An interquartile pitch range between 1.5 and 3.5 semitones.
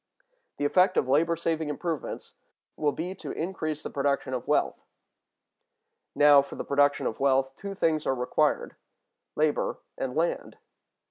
Yes: average, 3.0 semitones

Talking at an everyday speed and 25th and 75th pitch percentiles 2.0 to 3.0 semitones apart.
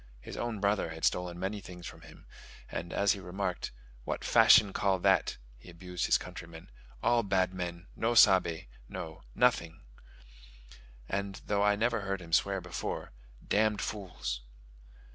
Yes: average, 150 wpm; average, 2.7 semitones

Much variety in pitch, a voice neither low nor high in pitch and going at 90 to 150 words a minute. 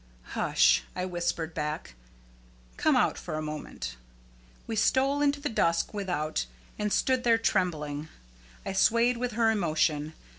Yes: wide, 7.0 semitones; medium, 180 Hz; average, 140 wpm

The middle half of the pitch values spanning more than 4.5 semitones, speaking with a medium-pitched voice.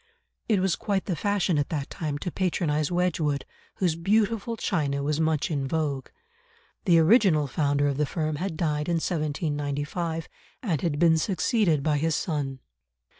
No: average, 3.6 semitones; medium, 160 Hz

